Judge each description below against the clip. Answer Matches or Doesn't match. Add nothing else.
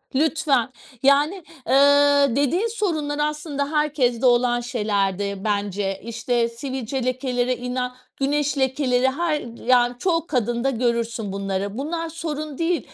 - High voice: Matches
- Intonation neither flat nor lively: Matches